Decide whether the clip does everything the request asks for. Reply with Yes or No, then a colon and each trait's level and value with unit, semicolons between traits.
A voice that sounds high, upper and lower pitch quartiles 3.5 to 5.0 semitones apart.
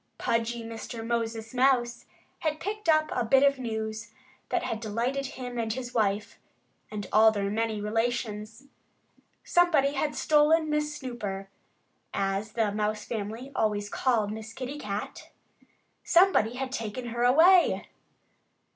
Yes: high, 235 Hz; average, 3.8 semitones